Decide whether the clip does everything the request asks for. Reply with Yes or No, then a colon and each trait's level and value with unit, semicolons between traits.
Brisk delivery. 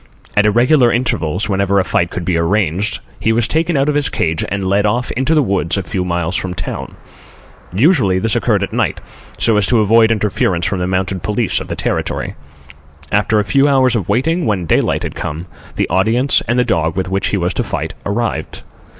Yes: fast, 210 wpm